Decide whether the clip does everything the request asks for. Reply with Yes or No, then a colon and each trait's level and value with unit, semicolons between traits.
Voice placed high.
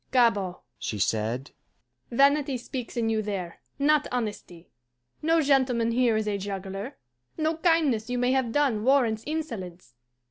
Yes: high, 235 Hz